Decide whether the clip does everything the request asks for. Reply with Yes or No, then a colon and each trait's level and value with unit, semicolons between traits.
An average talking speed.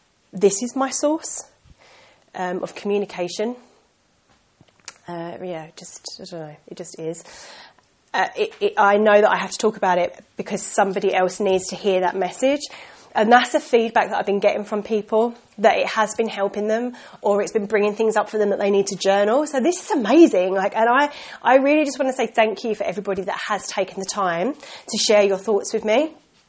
No: fast, 210 wpm